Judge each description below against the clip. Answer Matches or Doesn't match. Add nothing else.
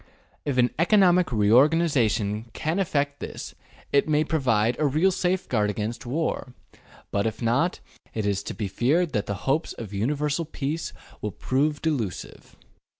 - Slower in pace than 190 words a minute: Matches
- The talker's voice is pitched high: Doesn't match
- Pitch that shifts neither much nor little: Doesn't match